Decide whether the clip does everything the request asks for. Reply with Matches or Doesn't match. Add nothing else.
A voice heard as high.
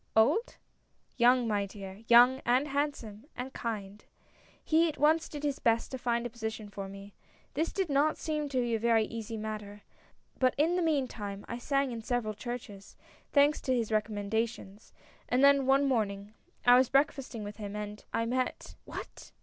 Matches